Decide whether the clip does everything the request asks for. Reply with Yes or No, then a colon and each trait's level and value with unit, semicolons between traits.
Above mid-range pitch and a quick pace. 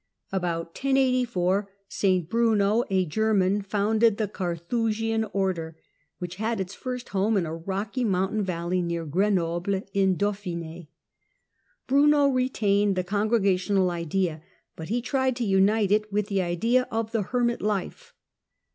No: high, 200 Hz; slow, 135 wpm